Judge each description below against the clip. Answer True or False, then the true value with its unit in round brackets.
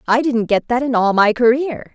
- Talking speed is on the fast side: True (245 wpm)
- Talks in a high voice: True (240 Hz)